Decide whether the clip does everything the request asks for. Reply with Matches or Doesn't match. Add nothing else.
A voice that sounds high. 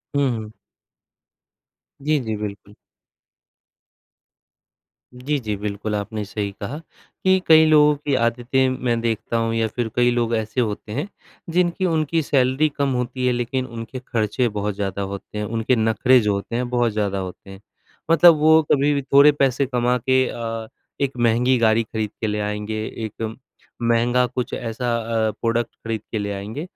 Doesn't match